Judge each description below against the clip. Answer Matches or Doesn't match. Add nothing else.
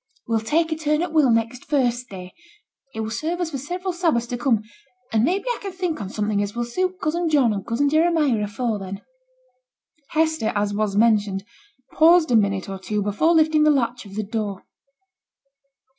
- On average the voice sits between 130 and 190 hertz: Doesn't match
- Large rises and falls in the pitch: Matches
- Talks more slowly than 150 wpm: Doesn't match